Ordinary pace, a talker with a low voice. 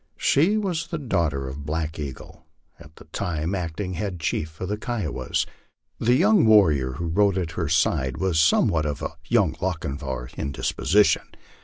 Yes: average, 170 wpm; very low, 85 Hz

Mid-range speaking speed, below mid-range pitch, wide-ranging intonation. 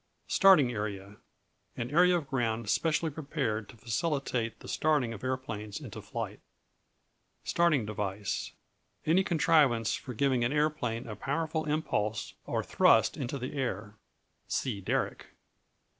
No: slow, 130 wpm; low, 125 Hz; wide, 5.8 semitones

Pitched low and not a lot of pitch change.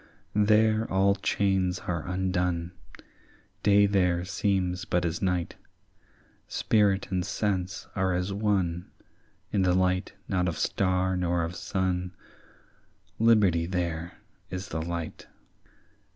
Yes: very low, 90 Hz; narrow, 1.9 semitones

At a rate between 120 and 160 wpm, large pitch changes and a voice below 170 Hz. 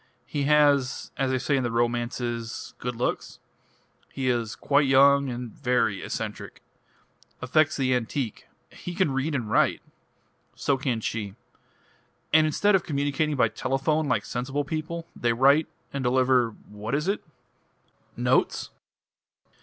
No: average, 140 wpm; average, 3.2 semitones; low, 135 Hz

